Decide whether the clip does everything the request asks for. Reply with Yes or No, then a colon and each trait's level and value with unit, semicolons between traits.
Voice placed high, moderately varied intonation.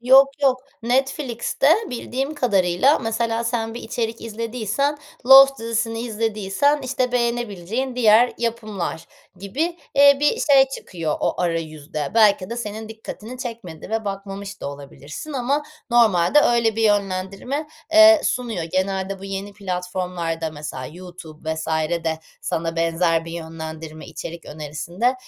No: high, 215 Hz; wide, 5.9 semitones